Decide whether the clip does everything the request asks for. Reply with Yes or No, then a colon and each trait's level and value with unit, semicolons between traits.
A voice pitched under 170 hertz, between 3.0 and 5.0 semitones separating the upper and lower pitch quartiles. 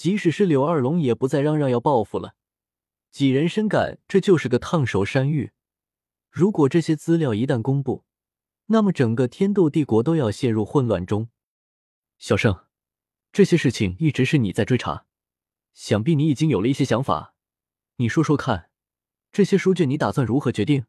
No: medium, 140 Hz; wide, 5.6 semitones